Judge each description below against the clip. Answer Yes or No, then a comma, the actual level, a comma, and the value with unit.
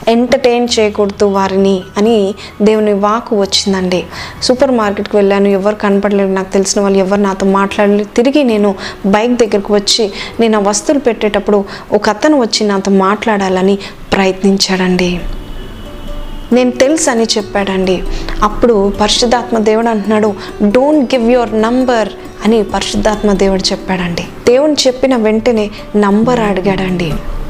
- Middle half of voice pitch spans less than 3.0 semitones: Yes, narrow, 2.6 semitones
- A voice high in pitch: Yes, high, 210 Hz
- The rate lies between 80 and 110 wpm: No, average, 120 wpm